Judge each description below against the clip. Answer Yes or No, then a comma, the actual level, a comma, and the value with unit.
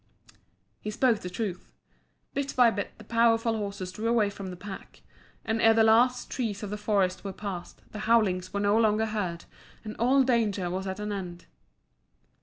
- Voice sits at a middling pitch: No, high, 210 Hz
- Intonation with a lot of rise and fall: No, average, 3.0 semitones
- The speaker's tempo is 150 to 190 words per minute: Yes, average, 185 wpm